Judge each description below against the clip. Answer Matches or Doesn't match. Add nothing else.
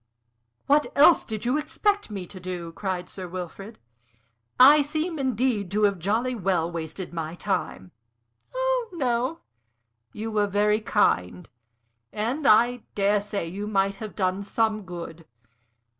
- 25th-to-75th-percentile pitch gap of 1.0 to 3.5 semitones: Doesn't match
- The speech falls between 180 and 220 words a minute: Doesn't match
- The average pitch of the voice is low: Doesn't match